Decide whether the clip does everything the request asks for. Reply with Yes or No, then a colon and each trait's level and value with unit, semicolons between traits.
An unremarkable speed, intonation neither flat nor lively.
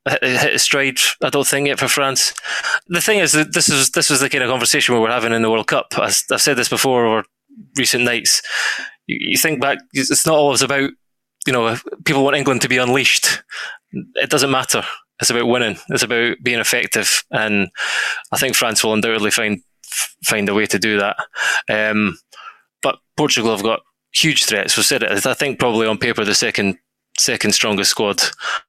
Yes: average, 195 wpm; average, 3.9 semitones